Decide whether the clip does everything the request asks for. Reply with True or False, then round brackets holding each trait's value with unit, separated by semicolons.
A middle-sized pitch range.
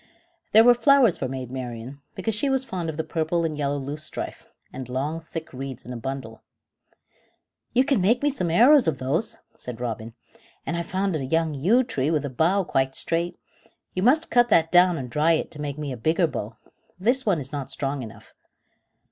False (6.3 semitones)